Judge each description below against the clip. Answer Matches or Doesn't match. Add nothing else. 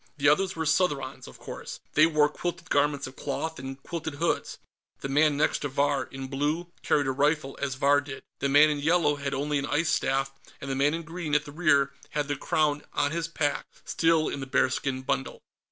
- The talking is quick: Matches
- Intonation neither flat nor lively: Doesn't match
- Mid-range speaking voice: Matches